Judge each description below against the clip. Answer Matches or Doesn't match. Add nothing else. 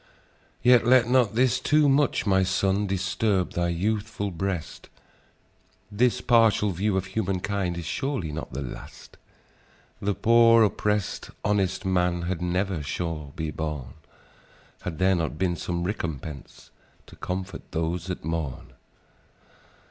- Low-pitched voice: Matches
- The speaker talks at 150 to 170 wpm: Doesn't match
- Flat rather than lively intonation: Doesn't match